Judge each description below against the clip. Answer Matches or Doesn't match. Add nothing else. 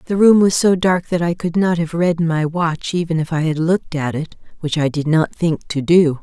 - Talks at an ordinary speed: Doesn't match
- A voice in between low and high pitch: Matches